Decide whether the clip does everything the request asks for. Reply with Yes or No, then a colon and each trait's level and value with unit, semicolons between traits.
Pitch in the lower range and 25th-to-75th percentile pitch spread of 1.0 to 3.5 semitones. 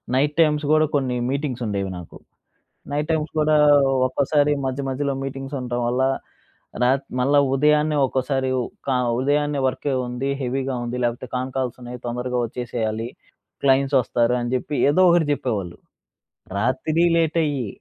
Yes: low, 130 Hz; average, 3.1 semitones